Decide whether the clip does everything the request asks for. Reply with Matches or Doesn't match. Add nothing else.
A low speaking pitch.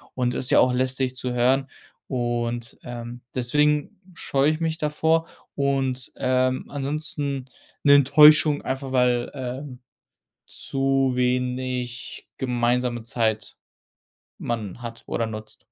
Matches